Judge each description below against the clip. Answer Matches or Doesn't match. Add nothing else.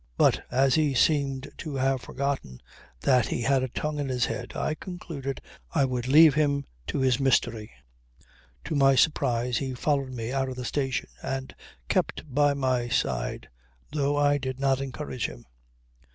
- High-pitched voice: Doesn't match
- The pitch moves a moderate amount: Doesn't match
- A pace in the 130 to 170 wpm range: Matches